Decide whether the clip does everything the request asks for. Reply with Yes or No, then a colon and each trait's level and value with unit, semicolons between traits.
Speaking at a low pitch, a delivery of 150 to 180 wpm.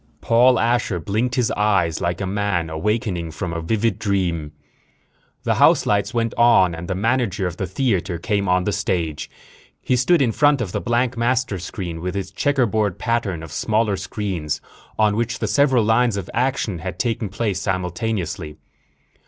Yes: low, 100 Hz; average, 175 wpm